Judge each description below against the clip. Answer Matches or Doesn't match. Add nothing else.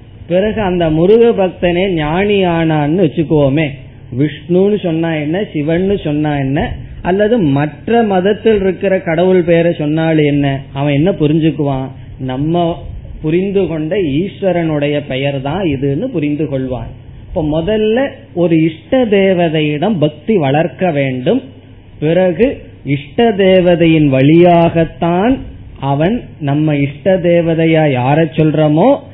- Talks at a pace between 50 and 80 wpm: Doesn't match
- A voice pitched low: Doesn't match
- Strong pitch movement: Doesn't match